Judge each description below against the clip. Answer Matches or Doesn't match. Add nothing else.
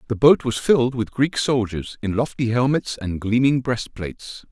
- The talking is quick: Doesn't match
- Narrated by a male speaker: Matches